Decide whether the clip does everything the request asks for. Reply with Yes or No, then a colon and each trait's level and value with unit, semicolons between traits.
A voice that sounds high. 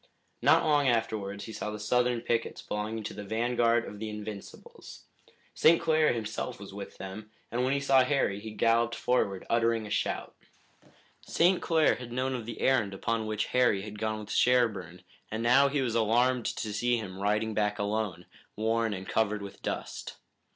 No: low, 110 Hz